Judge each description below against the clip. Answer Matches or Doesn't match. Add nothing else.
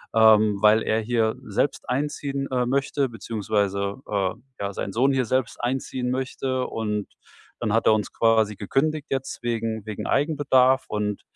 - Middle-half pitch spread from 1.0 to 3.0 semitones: Doesn't match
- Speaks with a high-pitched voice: Doesn't match